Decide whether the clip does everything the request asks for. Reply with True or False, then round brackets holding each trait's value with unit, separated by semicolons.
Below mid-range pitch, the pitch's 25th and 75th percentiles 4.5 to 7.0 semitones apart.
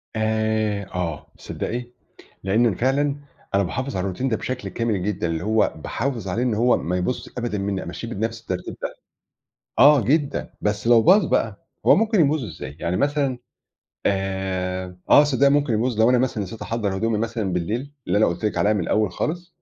True (110 Hz; 4.9 semitones)